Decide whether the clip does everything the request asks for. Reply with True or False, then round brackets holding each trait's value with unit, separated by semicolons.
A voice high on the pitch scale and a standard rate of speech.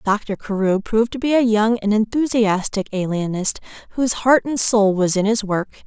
True (215 Hz; 185 wpm)